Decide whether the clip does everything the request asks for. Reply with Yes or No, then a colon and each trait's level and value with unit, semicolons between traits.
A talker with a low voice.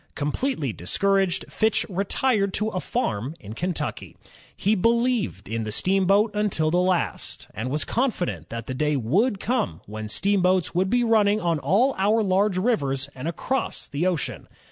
No: medium, 185 Hz